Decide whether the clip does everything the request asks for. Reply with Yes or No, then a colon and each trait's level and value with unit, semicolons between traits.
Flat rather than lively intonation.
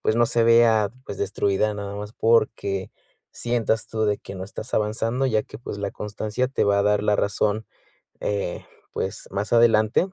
Yes: narrow, 2.1 semitones